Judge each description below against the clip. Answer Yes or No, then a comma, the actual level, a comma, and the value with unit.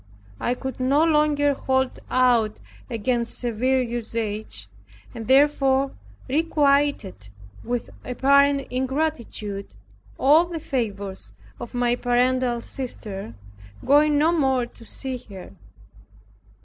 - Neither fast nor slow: No, slow, 100 wpm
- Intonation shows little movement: No, average, 3.2 semitones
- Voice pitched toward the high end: Yes, very high, 255 Hz